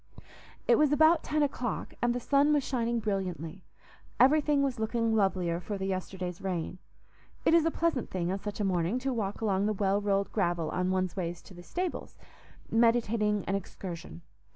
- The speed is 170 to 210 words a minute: Yes, average, 180 wpm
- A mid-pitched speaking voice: No, high, 205 Hz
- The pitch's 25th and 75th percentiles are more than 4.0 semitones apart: Yes, average, 5.2 semitones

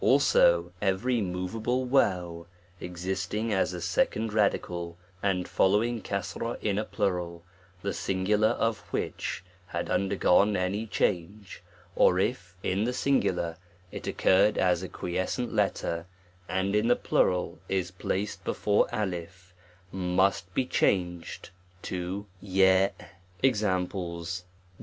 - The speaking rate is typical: No, slow, 130 wpm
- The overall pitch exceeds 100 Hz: No, very low, 95 Hz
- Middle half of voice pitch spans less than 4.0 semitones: Yes, average, 2.9 semitones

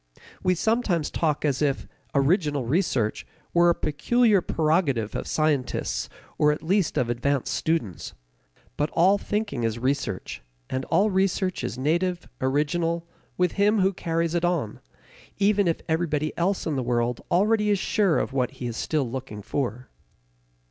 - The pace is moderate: Yes, average, 155 wpm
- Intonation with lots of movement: Yes, wide, 5.7 semitones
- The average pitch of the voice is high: No, medium, 155 Hz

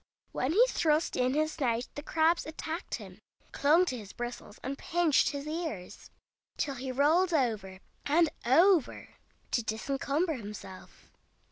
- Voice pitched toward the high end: Yes, very high, 285 Hz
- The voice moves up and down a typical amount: Yes, average, 5.0 semitones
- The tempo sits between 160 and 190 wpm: No, average, 140 wpm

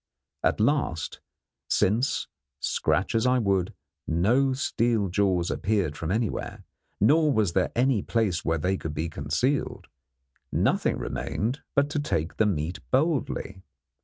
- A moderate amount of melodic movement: No, wide, 6.5 semitones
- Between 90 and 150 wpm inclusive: Yes, slow, 135 wpm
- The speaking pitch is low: Yes, low, 105 Hz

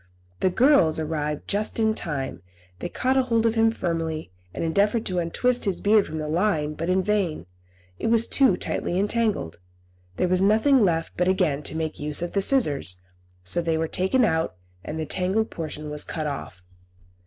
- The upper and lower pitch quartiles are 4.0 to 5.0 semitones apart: No, wide, 5.5 semitones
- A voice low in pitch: No, medium, 180 Hz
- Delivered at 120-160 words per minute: No, average, 185 wpm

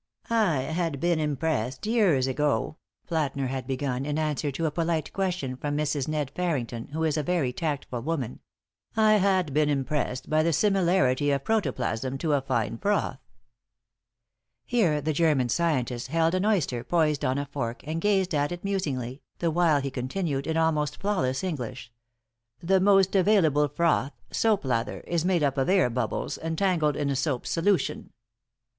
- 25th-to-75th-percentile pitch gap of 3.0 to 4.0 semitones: No, average, 4.5 semitones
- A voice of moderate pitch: Yes, medium, 150 Hz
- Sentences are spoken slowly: No, average, 165 wpm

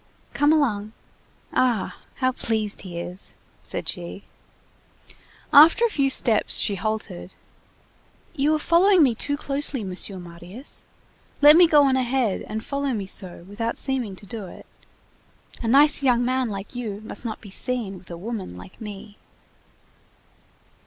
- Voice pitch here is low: No, high, 230 Hz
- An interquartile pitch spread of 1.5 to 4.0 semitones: No, wide, 5.6 semitones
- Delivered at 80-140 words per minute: No, average, 150 wpm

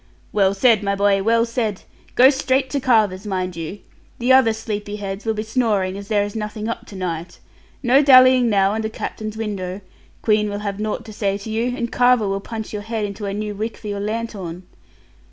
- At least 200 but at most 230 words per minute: Yes, fast, 205 wpm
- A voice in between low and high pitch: No, high, 215 Hz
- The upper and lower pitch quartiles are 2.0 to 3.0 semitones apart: Yes, narrow, 2.6 semitones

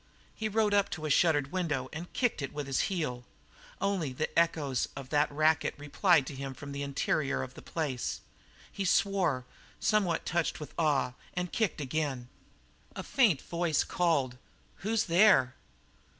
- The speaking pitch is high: No, medium, 155 Hz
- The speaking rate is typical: Yes, average, 160 wpm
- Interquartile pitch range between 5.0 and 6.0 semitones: No, average, 4.5 semitones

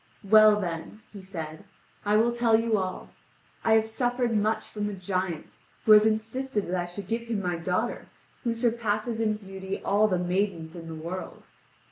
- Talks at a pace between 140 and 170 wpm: No, average, 180 wpm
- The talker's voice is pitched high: Yes, high, 210 Hz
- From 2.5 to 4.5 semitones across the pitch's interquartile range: Yes, average, 3.3 semitones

